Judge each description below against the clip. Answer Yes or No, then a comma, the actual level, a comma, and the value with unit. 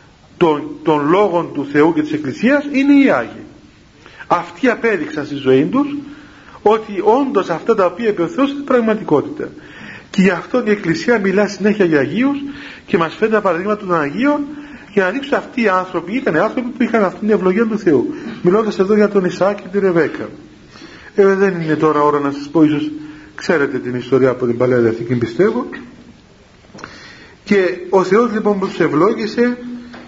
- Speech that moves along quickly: Yes, fast, 175 wpm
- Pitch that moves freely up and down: Yes, wide, 7.1 semitones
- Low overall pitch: No, high, 200 Hz